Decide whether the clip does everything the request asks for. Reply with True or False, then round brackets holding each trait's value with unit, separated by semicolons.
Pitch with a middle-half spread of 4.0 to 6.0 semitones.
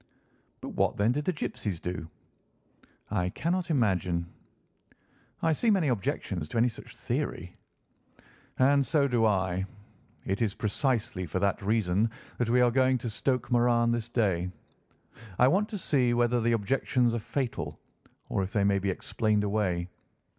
True (4.7 semitones)